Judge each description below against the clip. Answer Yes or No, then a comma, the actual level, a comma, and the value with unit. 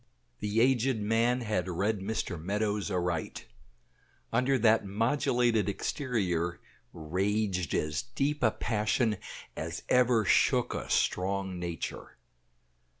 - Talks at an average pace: No, slow, 105 wpm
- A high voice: No, low, 105 Hz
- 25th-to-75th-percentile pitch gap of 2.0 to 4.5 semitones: Yes, average, 4.2 semitones